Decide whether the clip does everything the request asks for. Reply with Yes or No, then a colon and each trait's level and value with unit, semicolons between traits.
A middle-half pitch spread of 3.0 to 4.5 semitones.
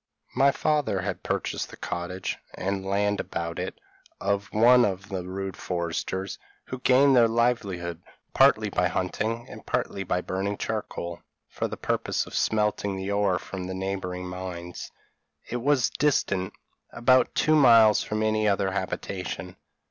Yes: average, 3.8 semitones